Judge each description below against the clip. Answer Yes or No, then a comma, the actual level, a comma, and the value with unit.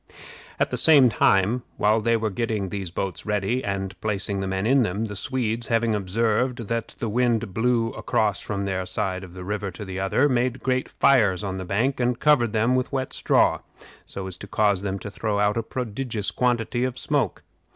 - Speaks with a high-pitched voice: No, low, 110 Hz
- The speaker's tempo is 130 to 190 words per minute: No, fast, 205 wpm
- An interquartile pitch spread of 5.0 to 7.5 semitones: No, average, 3.8 semitones